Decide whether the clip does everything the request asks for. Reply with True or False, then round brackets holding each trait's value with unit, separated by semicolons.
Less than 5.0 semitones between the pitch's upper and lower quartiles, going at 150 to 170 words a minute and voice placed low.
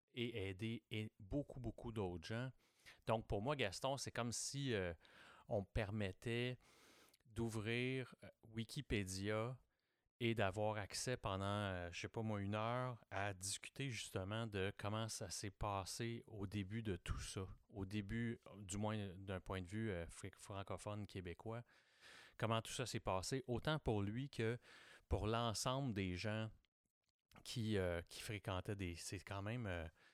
True (3.1 semitones; 155 wpm; 110 Hz)